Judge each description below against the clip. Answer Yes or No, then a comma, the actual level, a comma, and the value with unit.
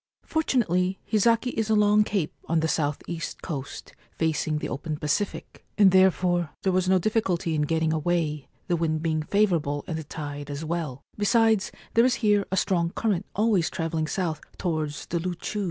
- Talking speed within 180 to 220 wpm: No, average, 170 wpm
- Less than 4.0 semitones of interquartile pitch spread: No, average, 4.5 semitones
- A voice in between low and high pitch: Yes, medium, 175 Hz